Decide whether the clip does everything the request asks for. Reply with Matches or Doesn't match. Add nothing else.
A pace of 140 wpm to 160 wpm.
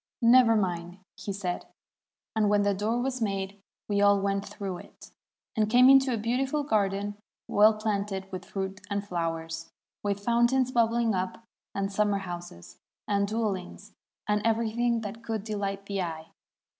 Matches